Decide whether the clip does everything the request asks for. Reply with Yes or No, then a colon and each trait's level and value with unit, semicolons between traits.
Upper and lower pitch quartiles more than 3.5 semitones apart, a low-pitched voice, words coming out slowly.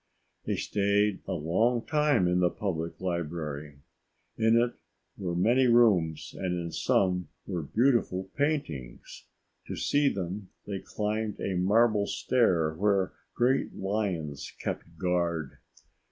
Yes: average, 4.7 semitones; very low, 95 Hz; slow, 125 wpm